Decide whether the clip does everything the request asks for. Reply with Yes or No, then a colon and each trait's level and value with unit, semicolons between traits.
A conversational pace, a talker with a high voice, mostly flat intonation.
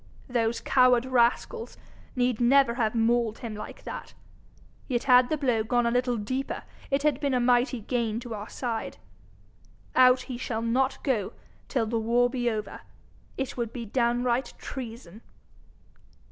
Yes: average, 155 wpm; high, 245 Hz; narrow, 1.9 semitones